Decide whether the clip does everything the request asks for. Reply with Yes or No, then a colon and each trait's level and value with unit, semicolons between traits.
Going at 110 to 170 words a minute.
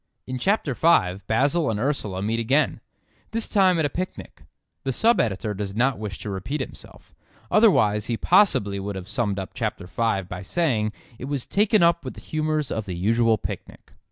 No: average, 185 wpm